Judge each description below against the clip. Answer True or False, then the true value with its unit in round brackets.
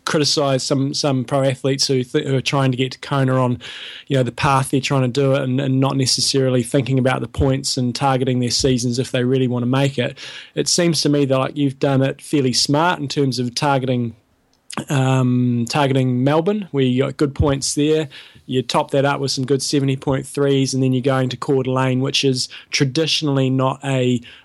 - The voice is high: False (135 Hz)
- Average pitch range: False (1.5 semitones)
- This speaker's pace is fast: True (215 wpm)